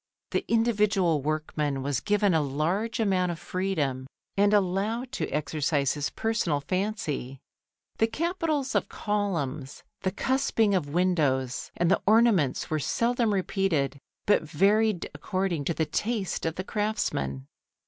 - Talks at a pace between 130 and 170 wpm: Yes, slow, 135 wpm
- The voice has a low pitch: No, medium, 185 Hz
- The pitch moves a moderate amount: No, wide, 6.1 semitones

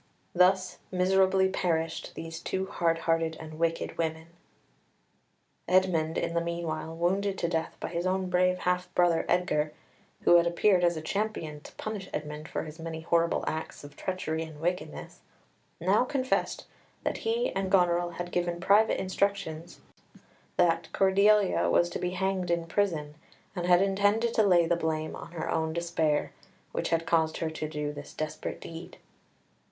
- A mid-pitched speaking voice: Yes, medium, 175 Hz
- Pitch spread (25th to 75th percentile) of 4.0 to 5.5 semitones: No, average, 2.7 semitones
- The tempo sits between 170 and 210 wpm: No, average, 160 wpm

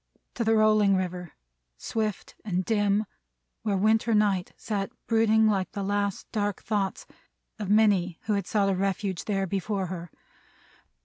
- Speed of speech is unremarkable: Yes, average, 145 wpm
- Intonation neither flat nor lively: No, narrow, 2.1 semitones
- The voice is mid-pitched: No, high, 205 Hz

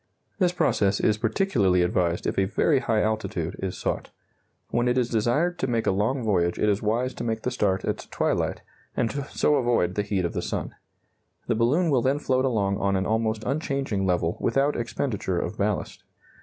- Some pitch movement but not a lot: Yes, average, 4.8 semitones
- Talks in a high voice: No, low, 110 Hz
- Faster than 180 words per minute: Yes, average, 195 wpm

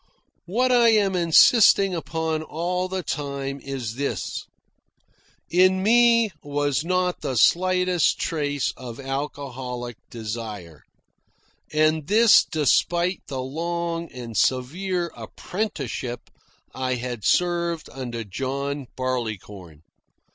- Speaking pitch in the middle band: Yes, medium, 145 Hz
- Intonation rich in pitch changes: Yes, wide, 5.9 semitones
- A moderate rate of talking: No, slow, 100 wpm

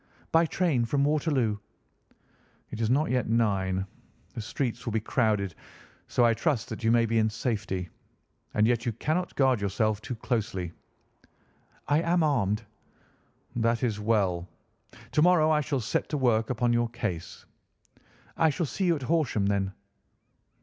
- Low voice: Yes, low, 115 Hz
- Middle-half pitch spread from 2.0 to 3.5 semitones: No, average, 5.1 semitones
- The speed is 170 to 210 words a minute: No, average, 155 wpm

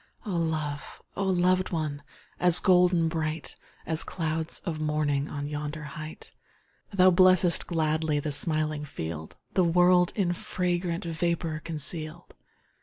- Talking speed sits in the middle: No, slow, 125 wpm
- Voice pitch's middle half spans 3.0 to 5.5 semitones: No, narrow, 2.6 semitones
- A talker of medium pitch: Yes, medium, 160 Hz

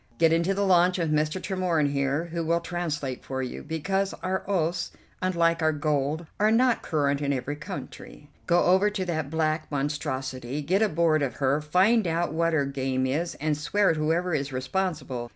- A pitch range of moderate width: Yes, average, 3.8 semitones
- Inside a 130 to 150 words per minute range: No, average, 185 wpm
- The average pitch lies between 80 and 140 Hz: No, medium, 160 Hz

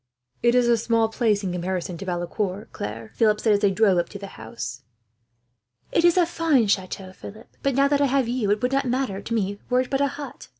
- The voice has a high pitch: Yes, high, 220 Hz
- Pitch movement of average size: Yes, average, 4.9 semitones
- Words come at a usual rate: No, fast, 240 wpm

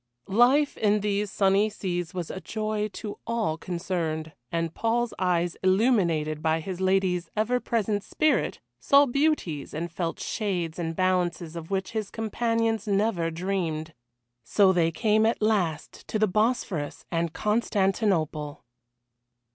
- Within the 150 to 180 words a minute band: No, slow, 135 wpm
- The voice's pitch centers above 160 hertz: Yes, high, 190 Hz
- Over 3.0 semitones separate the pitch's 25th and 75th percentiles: Yes, average, 4.5 semitones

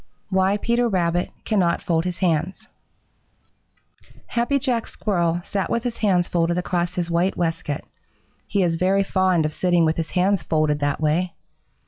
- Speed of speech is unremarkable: Yes, average, 160 wpm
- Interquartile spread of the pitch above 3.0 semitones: No, average, 2.7 semitones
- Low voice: No, medium, 180 Hz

